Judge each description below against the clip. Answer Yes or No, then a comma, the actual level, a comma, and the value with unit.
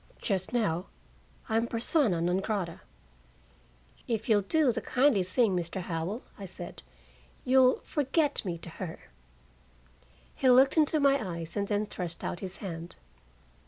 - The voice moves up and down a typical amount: No, wide, 6.1 semitones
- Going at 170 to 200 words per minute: No, average, 140 wpm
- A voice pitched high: Yes, high, 205 Hz